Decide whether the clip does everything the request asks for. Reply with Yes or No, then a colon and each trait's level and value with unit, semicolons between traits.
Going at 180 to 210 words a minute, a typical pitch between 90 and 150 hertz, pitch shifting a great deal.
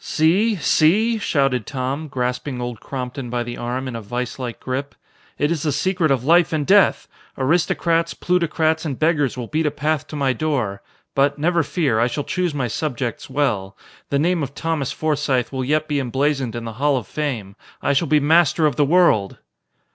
No: average, 190 wpm; medium, 140 Hz; average, 3.9 semitones